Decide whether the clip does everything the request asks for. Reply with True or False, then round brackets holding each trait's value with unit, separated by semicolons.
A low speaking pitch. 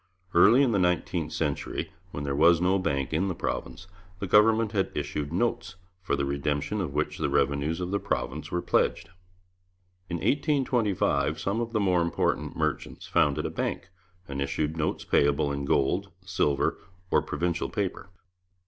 True (85 Hz)